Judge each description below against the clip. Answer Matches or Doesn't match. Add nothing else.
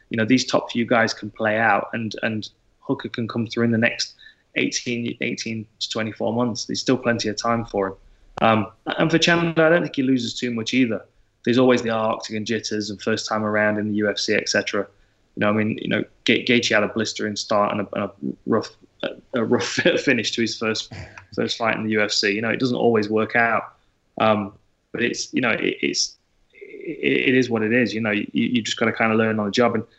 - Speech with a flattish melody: Matches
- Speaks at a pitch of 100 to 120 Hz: Matches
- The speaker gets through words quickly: Matches